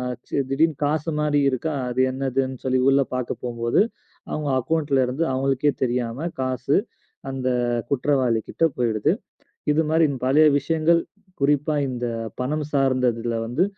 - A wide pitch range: No, average, 3.1 semitones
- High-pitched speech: No, low, 135 Hz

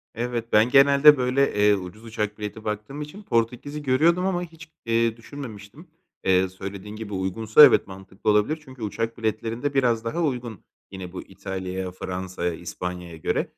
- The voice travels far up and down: Yes, wide, 5.9 semitones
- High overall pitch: No, low, 110 Hz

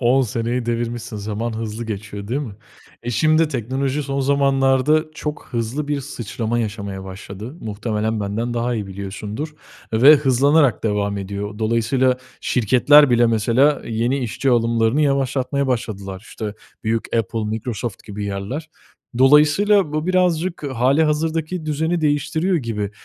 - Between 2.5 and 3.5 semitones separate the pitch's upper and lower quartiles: No, average, 4.9 semitones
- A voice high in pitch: No, low, 120 Hz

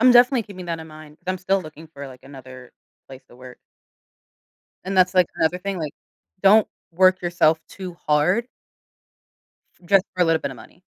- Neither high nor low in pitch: Yes, medium, 175 Hz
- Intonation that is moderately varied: Yes, average, 4.1 semitones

